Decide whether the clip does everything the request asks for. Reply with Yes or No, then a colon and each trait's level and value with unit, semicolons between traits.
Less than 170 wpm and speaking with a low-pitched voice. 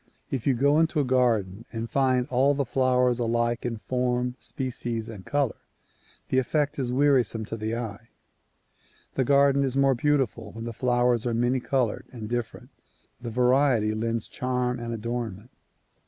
Yes: average, 160 wpm; low, 125 Hz